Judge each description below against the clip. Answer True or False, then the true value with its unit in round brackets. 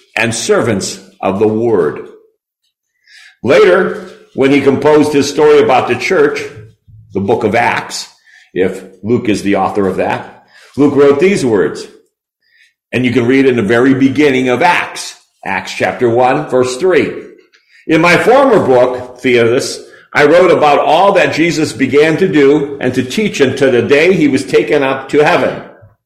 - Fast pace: False (160 wpm)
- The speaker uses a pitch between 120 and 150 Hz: True (140 Hz)